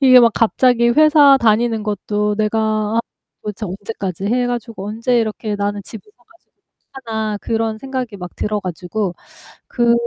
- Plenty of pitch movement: No, narrow, 2.6 semitones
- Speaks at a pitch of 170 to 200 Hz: No, high, 220 Hz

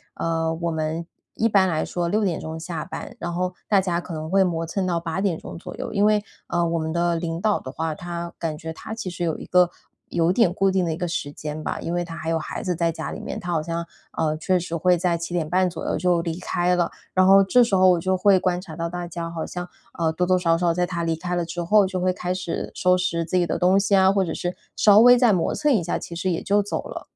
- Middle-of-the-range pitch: Yes, medium, 175 Hz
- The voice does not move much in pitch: Yes, narrow, 2.0 semitones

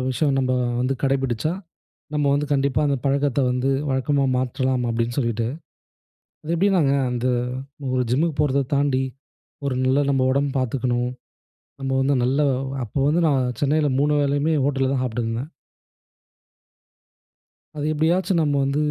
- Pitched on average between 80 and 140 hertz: Yes, low, 135 Hz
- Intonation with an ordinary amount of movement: No, narrow, 2.2 semitones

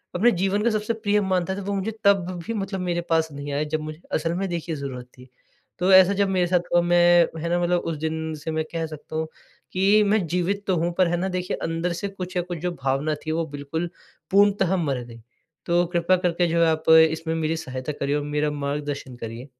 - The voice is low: No, medium, 170 Hz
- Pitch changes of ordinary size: Yes, average, 3.3 semitones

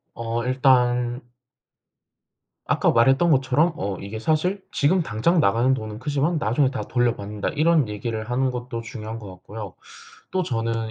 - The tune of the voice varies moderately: Yes, average, 4.0 semitones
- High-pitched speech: No, low, 120 Hz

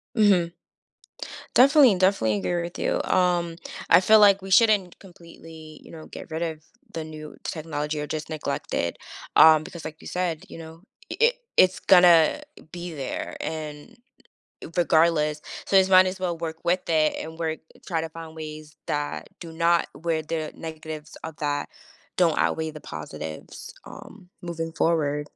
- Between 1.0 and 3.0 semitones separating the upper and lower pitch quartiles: Yes, narrow, 2.4 semitones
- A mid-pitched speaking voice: Yes, medium, 165 Hz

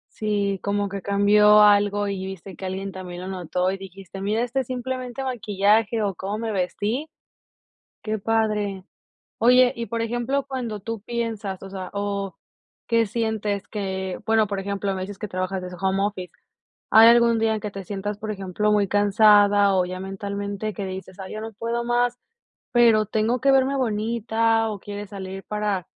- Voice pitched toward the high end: Yes, high, 205 Hz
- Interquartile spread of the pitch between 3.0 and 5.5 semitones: No, narrow, 2.6 semitones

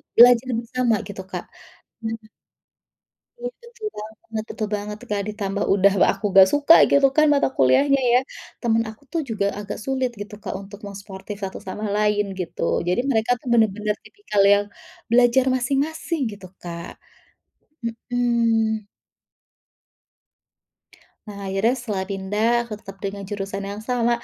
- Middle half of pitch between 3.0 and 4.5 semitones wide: Yes, average, 3.5 semitones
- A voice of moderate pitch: No, high, 215 Hz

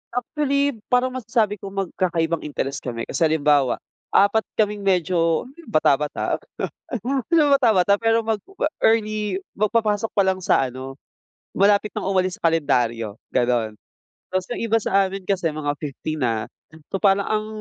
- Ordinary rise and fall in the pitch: No, wide, 6.3 semitones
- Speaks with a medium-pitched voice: No, high, 195 Hz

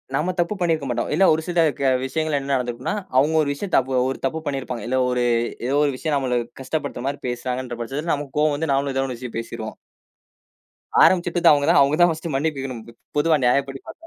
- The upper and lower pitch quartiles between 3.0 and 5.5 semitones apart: Yes, average, 3.6 semitones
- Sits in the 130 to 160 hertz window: Yes, medium, 140 Hz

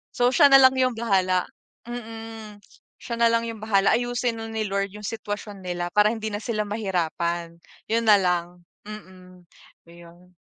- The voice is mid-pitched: No, high, 210 Hz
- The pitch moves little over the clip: No, average, 3.9 semitones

